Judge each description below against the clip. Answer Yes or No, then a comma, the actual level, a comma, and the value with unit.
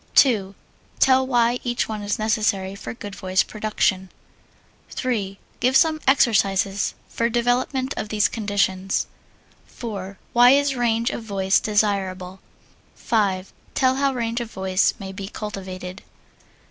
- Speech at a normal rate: No, slow, 130 wpm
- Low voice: No, high, 215 Hz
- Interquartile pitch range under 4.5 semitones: Yes, average, 3.9 semitones